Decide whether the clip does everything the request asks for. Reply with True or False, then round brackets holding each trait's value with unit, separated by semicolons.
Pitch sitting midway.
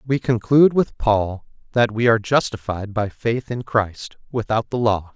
False (115 Hz)